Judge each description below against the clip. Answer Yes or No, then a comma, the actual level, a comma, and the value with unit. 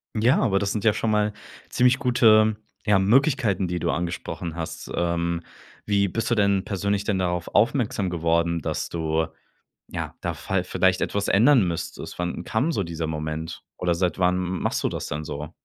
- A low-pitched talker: Yes, very low, 95 Hz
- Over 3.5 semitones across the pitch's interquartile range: Yes, average, 4.1 semitones